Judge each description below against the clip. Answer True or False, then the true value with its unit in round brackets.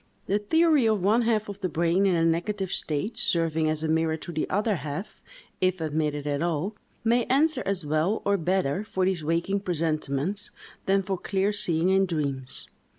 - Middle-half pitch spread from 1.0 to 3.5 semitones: False (4.2 semitones)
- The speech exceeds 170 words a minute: True (185 wpm)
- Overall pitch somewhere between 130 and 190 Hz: True (185 Hz)